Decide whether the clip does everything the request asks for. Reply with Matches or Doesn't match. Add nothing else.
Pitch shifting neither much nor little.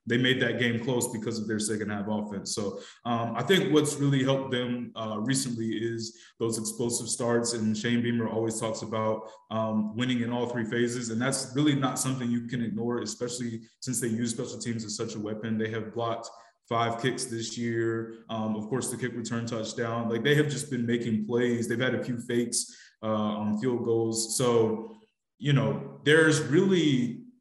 Doesn't match